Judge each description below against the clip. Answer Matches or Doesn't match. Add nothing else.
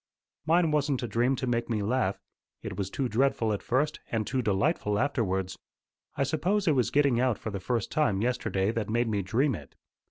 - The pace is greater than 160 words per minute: Matches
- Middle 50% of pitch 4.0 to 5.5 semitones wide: Matches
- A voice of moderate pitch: Doesn't match